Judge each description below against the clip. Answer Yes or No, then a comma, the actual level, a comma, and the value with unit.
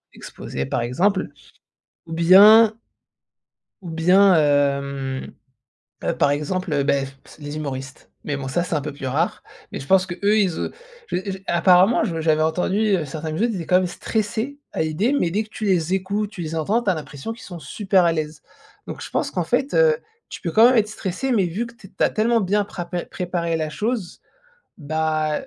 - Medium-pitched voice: Yes, medium, 175 Hz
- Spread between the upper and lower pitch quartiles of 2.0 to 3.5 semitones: No, average, 4.9 semitones